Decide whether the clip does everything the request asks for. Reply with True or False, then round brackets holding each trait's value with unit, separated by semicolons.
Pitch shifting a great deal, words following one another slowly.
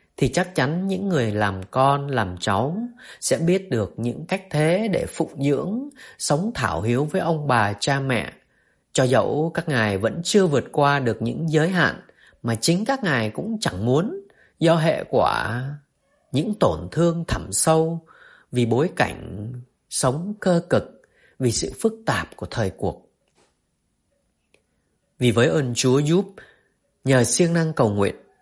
True (6.8 semitones; 160 wpm)